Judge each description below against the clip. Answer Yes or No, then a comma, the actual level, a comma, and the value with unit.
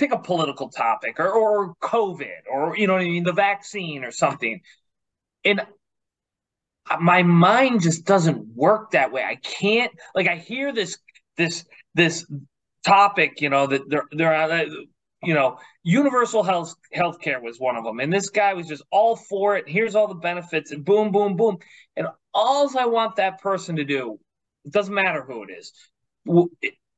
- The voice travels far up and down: No, average, 4.6 semitones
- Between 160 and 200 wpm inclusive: Yes, average, 180 wpm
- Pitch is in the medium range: Yes, medium, 180 Hz